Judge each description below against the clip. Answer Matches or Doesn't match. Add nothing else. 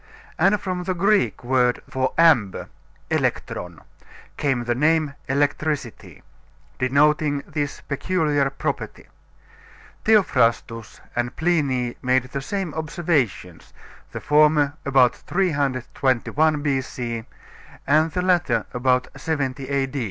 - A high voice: Doesn't match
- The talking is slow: Matches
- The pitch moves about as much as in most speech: Matches